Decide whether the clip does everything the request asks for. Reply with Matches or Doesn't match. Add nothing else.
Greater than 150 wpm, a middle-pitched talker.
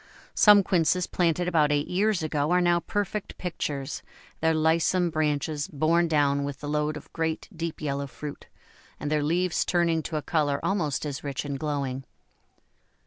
Matches